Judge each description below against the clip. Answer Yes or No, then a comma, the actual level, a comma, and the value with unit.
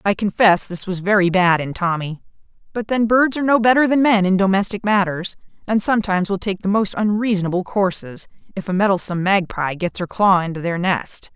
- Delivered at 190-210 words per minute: Yes, average, 195 wpm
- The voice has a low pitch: No, high, 195 Hz